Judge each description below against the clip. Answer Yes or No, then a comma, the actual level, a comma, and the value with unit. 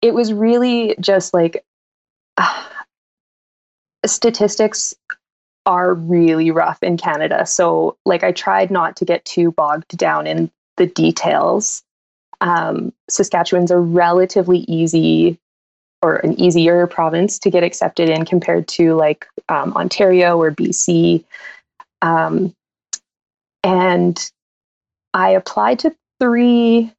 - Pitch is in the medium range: Yes, medium, 175 Hz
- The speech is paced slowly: Yes, slow, 115 wpm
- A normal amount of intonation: Yes, average, 3.4 semitones